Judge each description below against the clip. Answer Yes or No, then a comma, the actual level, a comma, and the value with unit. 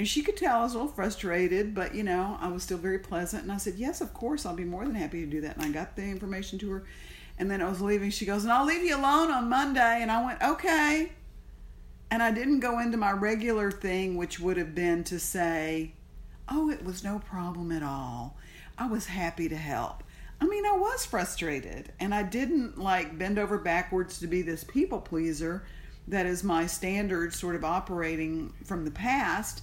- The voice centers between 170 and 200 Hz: Yes, high, 190 Hz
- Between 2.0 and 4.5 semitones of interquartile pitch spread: No, average, 5.3 semitones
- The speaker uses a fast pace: Yes, fast, 220 wpm